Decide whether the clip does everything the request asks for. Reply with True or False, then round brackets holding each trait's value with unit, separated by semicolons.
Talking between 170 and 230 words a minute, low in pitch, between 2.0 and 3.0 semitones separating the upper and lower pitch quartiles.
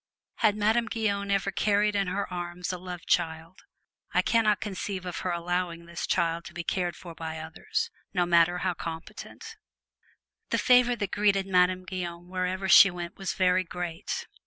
False (180 wpm; 180 Hz; 2.6 semitones)